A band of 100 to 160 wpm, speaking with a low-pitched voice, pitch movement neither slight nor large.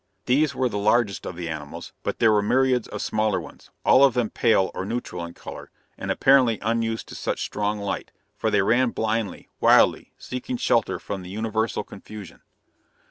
No: average, 185 wpm; low, 110 Hz; average, 3.2 semitones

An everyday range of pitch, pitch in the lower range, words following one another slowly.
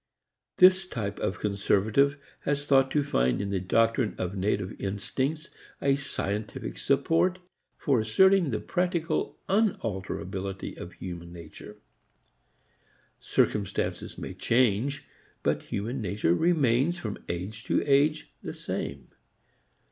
No: wide, 6.8 semitones; low, 115 Hz; slow, 115 wpm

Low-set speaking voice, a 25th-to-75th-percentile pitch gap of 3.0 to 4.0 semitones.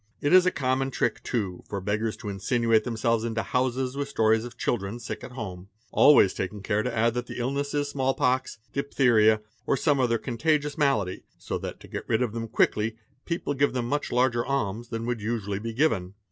Yes: low, 120 Hz; average, 3.6 semitones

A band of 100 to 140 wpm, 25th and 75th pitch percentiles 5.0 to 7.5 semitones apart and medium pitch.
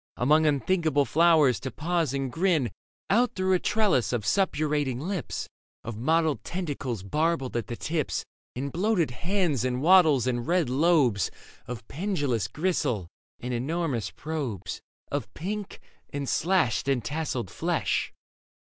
Yes: slow, 135 wpm; wide, 5.5 semitones; medium, 145 Hz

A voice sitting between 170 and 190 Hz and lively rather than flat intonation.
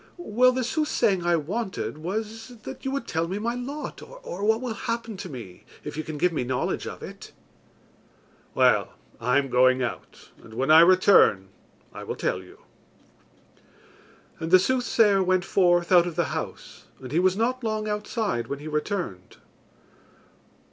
Yes: medium, 185 Hz; wide, 6.9 semitones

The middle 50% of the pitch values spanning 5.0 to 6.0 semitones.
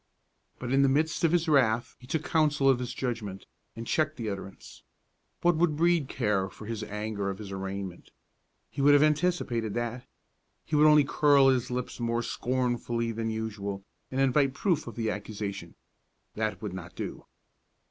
Yes: average, 5.3 semitones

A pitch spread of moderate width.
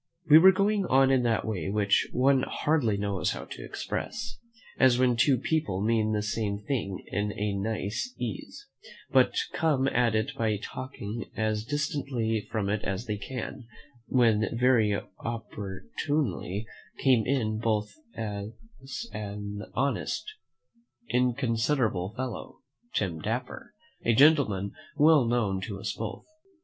Yes: average, 4.2 semitones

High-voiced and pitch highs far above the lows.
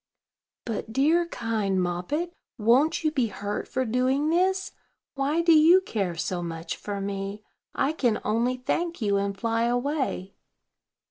Yes: high, 240 Hz; wide, 7.2 semitones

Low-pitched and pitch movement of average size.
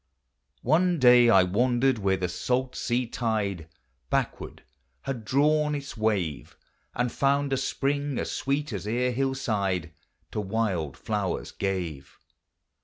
No: low, 120 Hz; wide, 5.7 semitones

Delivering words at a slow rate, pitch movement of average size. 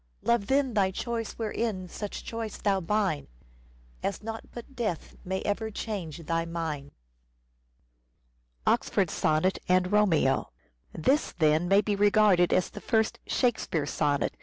Yes: slow, 130 wpm; average, 4.8 semitones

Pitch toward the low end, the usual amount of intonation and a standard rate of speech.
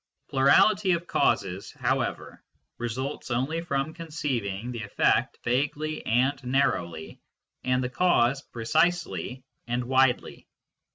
No: low, 130 Hz; average, 3.9 semitones; slow, 105 wpm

